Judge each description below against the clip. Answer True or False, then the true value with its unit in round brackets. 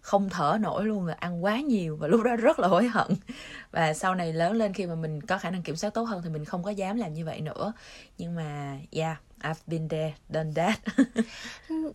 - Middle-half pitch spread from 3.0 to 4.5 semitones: False (5.2 semitones)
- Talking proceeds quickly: False (235 wpm)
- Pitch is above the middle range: False (180 Hz)